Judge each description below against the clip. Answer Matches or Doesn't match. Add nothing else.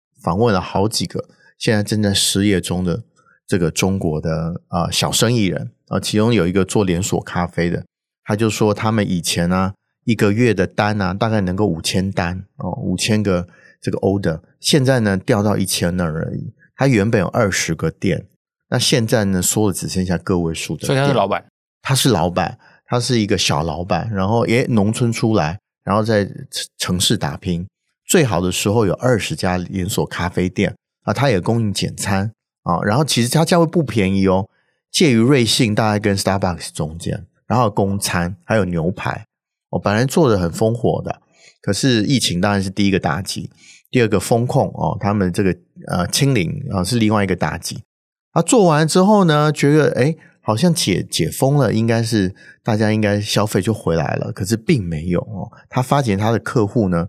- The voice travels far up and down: Doesn't match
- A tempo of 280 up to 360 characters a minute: Matches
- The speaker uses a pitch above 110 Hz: Doesn't match